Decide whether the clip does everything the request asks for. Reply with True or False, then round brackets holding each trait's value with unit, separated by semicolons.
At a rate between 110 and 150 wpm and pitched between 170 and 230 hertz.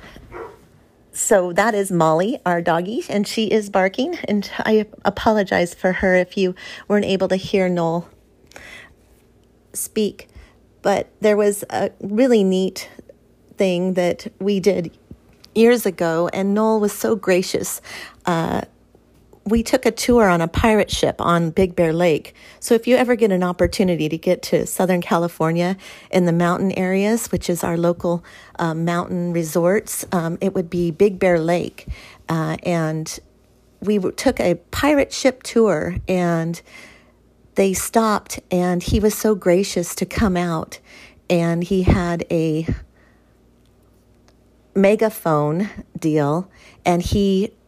True (140 wpm; 185 Hz)